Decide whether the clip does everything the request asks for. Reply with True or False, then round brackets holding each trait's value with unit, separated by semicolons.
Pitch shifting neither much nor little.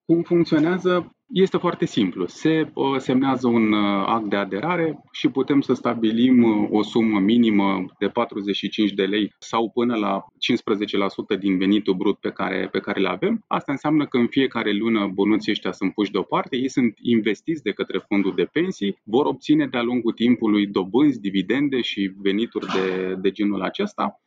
False (6.0 semitones)